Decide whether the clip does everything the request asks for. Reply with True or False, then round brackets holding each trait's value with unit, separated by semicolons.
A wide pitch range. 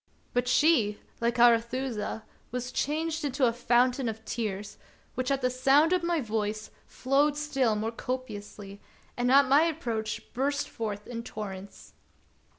False (3.9 semitones)